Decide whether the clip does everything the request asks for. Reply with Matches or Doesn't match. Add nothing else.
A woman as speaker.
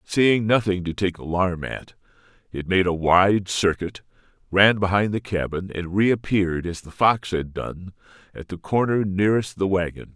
Doesn't match